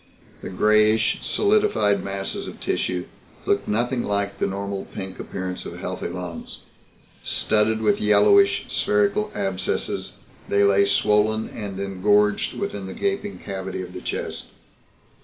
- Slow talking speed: Yes, slow, 130 wpm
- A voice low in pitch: Yes, low, 100 Hz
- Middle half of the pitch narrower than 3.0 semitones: Yes, narrow, 2.4 semitones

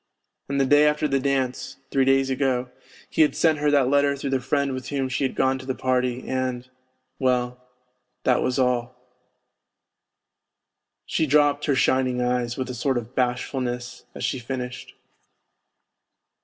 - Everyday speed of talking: Yes, average, 160 wpm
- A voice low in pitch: Yes, low, 130 Hz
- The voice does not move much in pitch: Yes, narrow, 1.7 semitones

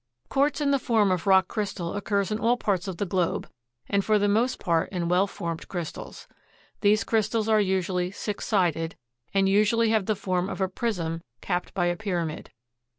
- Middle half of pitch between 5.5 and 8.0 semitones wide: No, average, 3.3 semitones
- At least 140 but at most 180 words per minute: No, average, 190 wpm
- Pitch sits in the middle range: No, high, 195 Hz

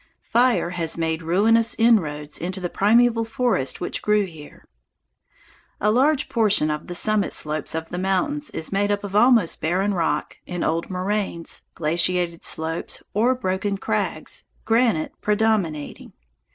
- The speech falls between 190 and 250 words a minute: No, average, 140 wpm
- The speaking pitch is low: No, high, 195 Hz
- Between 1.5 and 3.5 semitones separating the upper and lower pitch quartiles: No, average, 5.1 semitones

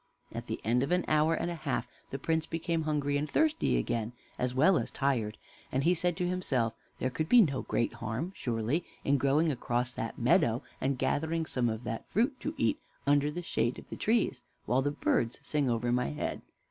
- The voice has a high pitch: No, medium, 140 Hz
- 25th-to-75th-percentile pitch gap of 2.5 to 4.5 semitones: No, average, 5.3 semitones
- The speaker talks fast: Yes, fast, 210 wpm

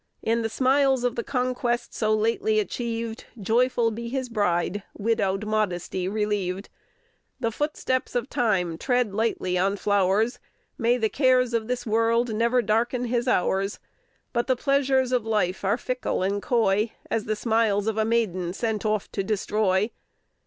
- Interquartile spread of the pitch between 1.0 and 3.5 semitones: Yes, average, 3.1 semitones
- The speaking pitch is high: Yes, high, 225 Hz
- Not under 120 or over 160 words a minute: Yes, average, 155 wpm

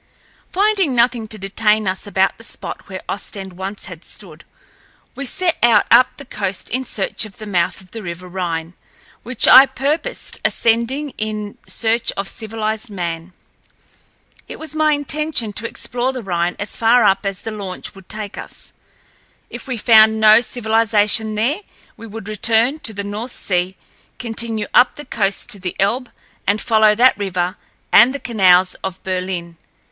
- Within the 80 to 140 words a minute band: No, average, 165 wpm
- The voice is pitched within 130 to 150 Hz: No, high, 215 Hz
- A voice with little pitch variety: No, average, 3.8 semitones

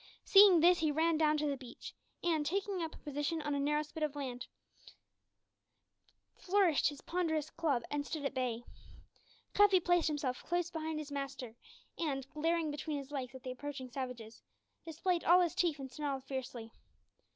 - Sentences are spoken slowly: No, average, 175 wpm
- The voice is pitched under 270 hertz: No, very high, 300 Hz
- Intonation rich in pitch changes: No, average, 3.5 semitones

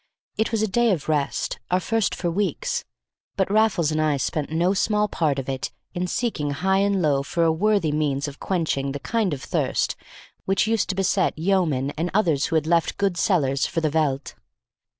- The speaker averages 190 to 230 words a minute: Yes, average, 200 wpm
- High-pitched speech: No, medium, 170 Hz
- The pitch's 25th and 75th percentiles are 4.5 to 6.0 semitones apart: Yes, average, 5.2 semitones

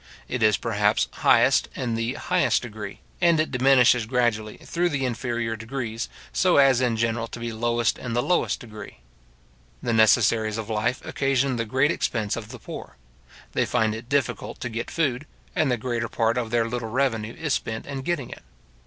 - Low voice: Yes, low, 120 Hz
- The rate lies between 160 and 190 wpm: Yes, average, 185 wpm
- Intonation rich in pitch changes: No, average, 2.8 semitones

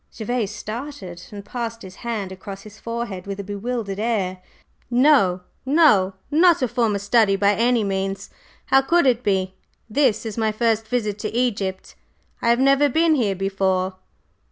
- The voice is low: No, high, 215 Hz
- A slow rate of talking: No, average, 160 wpm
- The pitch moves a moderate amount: Yes, average, 3.9 semitones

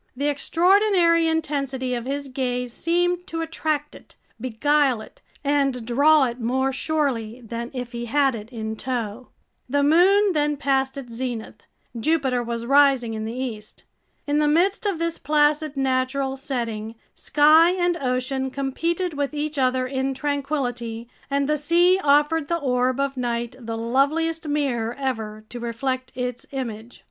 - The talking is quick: No, average, 155 wpm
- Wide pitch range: No, average, 3.6 semitones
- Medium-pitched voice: No, very high, 270 Hz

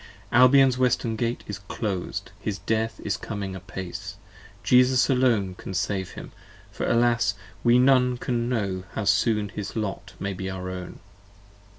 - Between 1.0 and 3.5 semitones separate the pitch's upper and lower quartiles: No, average, 4.3 semitones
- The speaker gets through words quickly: No, average, 150 wpm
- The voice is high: No, low, 105 Hz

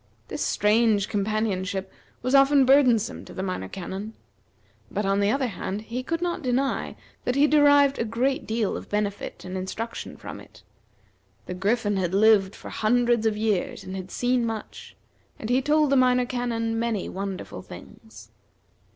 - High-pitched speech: Yes, high, 225 Hz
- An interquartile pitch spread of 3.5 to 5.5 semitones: Yes, average, 4.0 semitones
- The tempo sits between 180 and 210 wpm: No, average, 165 wpm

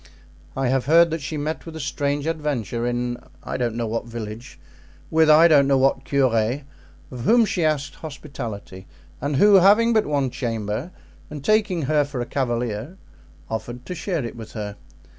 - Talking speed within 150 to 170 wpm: No, average, 180 wpm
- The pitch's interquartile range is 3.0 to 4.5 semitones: No, average, 4.9 semitones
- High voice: No, medium, 140 Hz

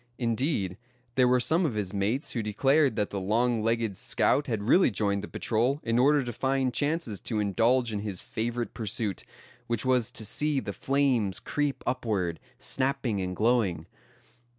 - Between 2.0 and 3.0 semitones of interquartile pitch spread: No, average, 4.1 semitones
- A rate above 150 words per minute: Yes, average, 170 wpm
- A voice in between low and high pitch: No, low, 115 Hz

